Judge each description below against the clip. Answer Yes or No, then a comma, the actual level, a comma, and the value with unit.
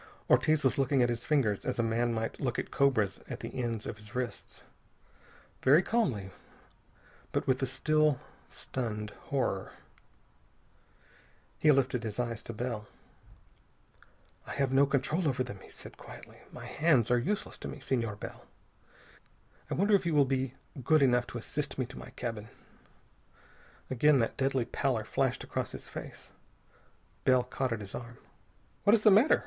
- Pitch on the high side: No, low, 130 Hz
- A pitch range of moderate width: Yes, average, 3.3 semitones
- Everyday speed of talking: Yes, average, 165 wpm